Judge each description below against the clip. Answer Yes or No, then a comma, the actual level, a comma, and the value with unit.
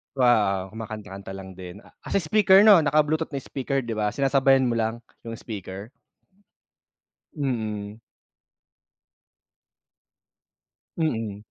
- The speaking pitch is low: Yes, low, 115 Hz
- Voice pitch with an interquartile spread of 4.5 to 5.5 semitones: Yes, average, 5.2 semitones